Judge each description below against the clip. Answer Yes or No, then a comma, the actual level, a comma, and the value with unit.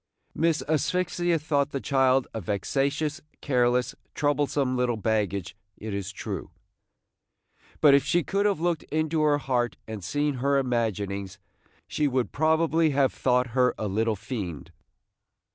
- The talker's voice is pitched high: No, low, 135 Hz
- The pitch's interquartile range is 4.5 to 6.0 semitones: Yes, average, 5.1 semitones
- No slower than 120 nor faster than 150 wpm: Yes, average, 140 wpm